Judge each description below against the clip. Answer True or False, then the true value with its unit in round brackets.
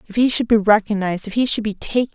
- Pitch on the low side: False (215 Hz)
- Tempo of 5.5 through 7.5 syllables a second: True (7.0 syllables/s)